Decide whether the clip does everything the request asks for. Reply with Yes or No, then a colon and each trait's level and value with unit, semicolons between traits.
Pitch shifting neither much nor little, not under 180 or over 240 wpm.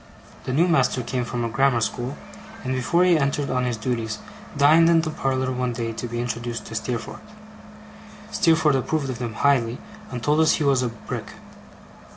Yes: average, 3.5 semitones; average, 190 wpm